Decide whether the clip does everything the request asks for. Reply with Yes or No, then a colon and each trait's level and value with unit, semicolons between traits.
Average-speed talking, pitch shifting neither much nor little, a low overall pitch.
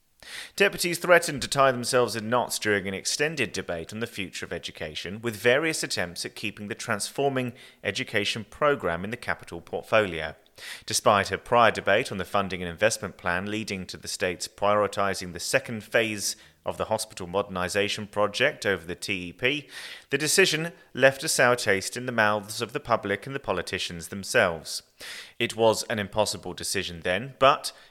Yes: average, 170 wpm; average, 4.2 semitones; low, 105 Hz